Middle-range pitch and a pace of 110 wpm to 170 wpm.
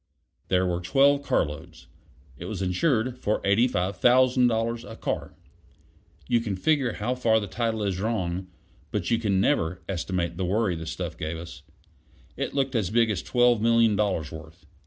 No: low, 105 Hz; average, 160 wpm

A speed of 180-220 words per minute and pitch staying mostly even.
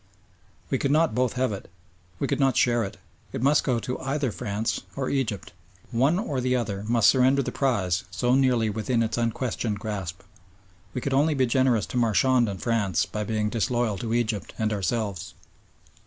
No: average, 185 wpm; average, 3.5 semitones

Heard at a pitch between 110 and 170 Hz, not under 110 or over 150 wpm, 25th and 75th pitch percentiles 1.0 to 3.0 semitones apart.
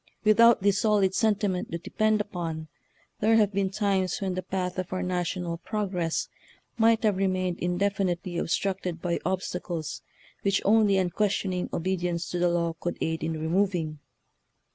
No: medium, 185 Hz; average, 145 wpm; narrow, 2.6 semitones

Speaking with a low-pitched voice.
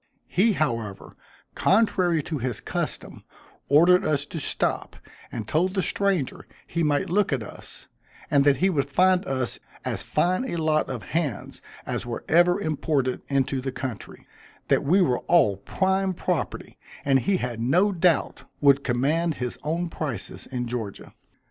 No: medium, 155 Hz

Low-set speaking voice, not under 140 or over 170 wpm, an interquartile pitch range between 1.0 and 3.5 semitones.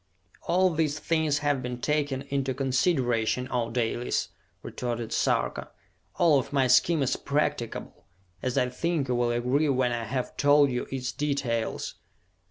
Yes: low, 130 Hz; average, 150 wpm; average, 3.0 semitones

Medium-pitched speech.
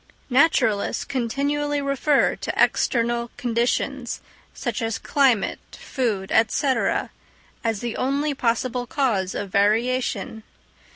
No: high, 245 Hz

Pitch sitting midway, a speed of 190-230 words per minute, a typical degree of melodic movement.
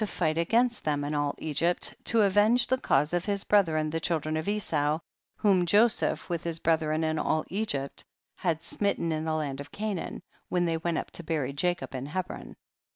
Yes: medium, 165 Hz; average, 195 wpm; average, 4.1 semitones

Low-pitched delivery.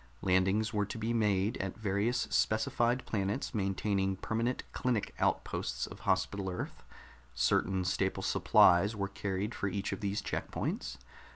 Yes: low, 100 Hz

